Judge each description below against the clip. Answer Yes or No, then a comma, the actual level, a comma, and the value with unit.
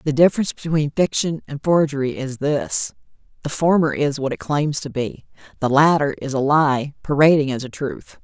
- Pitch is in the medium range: Yes, medium, 145 Hz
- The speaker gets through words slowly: No, average, 180 wpm